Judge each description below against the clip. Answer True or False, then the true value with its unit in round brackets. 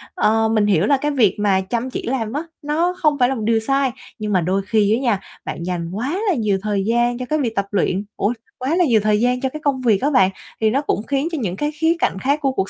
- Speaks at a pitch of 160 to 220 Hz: False (235 Hz)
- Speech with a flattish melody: False (4.9 semitones)